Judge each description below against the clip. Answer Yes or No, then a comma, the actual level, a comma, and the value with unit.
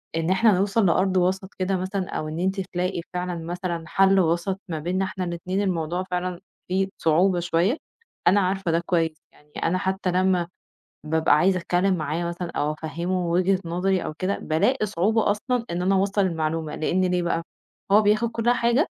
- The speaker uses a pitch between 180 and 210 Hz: Yes, medium, 185 Hz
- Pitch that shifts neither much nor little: No, narrow, 2.2 semitones